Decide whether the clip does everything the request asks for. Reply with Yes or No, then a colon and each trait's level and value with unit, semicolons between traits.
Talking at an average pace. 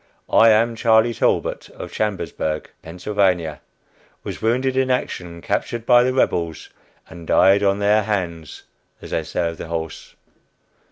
Yes: average, 145 wpm